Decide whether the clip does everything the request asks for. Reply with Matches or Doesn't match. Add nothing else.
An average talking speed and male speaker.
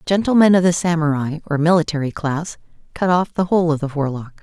Doesn't match